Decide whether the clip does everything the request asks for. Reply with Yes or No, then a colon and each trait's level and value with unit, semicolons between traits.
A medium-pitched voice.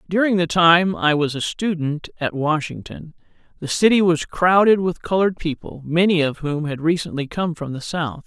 Yes: medium, 165 Hz